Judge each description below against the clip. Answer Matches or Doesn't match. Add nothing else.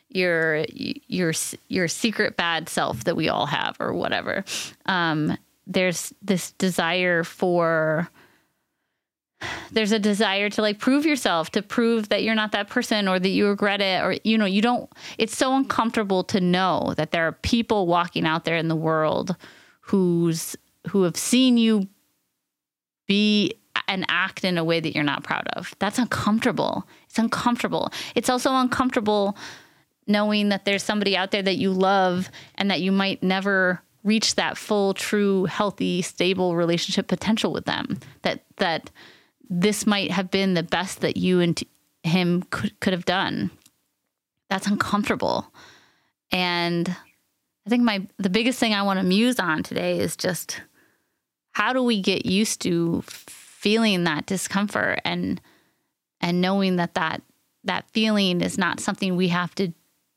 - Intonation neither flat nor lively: Matches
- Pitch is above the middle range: Matches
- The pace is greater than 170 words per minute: Doesn't match